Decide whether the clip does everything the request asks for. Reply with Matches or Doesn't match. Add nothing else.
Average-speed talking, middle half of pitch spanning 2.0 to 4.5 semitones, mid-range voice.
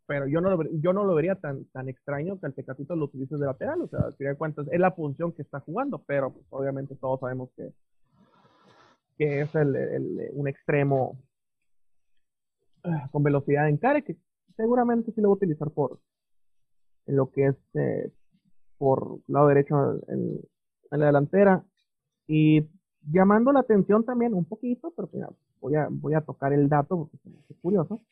Doesn't match